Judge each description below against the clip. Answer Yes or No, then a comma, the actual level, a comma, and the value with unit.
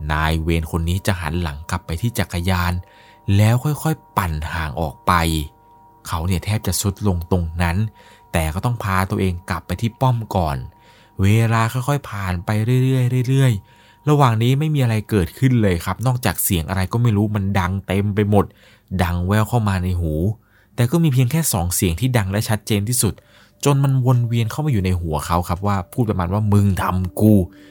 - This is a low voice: Yes, low, 100 Hz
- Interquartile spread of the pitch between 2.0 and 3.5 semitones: No, average, 4.6 semitones